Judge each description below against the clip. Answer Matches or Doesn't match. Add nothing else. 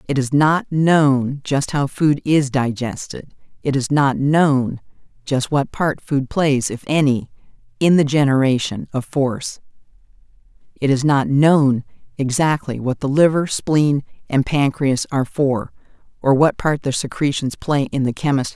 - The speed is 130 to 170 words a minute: Matches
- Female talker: Matches